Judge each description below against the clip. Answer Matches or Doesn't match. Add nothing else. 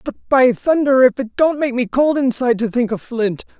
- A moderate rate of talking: Doesn't match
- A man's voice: Doesn't match